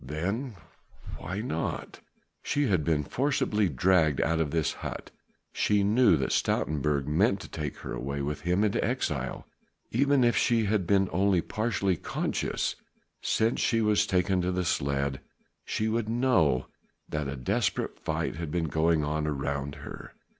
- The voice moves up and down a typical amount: No, wide, 6.2 semitones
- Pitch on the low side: Yes, very low, 90 Hz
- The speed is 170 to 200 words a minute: No, average, 155 wpm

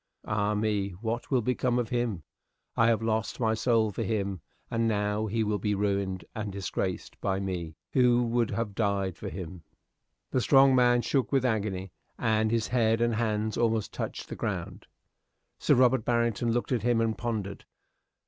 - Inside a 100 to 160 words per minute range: No, average, 175 wpm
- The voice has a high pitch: No, low, 110 Hz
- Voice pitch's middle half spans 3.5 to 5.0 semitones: No, average, 2.7 semitones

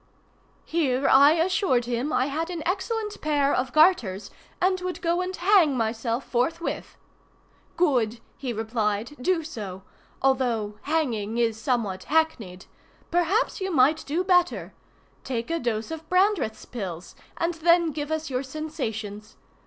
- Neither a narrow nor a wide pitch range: No, wide, 6.6 semitones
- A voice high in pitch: Yes, very high, 285 Hz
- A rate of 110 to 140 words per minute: Yes, slow, 135 wpm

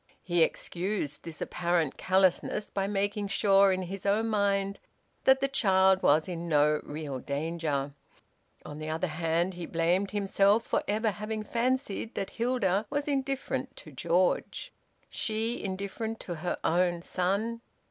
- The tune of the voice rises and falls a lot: No, average, 4.0 semitones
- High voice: Yes, high, 195 Hz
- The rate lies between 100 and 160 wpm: Yes, average, 145 wpm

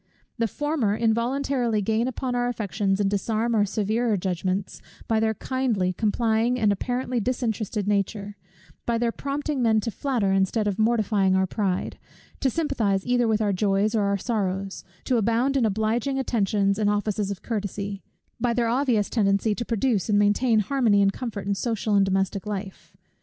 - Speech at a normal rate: Yes, average, 170 wpm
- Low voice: No, high, 215 Hz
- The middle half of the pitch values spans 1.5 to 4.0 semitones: Yes, average, 3.1 semitones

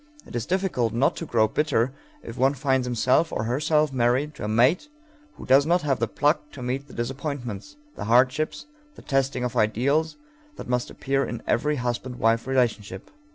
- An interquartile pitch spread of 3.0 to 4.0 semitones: Yes, average, 3.6 semitones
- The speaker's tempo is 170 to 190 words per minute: Yes, average, 185 wpm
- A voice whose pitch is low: Yes, low, 130 Hz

